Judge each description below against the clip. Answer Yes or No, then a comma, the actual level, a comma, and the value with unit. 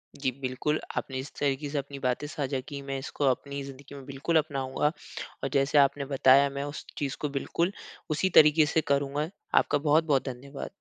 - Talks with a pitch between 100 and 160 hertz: Yes, medium, 140 Hz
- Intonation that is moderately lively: No, narrow, 1.4 semitones